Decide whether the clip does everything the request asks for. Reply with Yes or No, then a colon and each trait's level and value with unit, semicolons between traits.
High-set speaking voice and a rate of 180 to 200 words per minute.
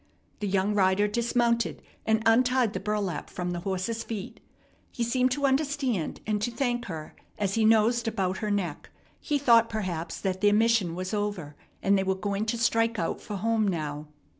Yes: high, 210 Hz; average, 185 wpm